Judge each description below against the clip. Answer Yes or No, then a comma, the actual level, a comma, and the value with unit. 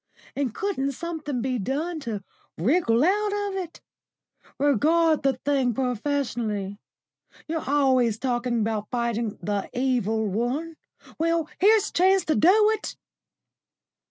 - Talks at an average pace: No, slow, 125 wpm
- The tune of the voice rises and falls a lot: Yes, wide, 5.9 semitones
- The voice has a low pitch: No, very high, 270 Hz